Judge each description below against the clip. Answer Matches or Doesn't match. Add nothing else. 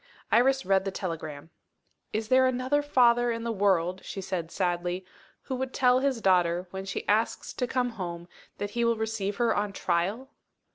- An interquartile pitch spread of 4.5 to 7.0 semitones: Matches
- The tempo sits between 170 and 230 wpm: Matches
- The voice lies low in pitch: Doesn't match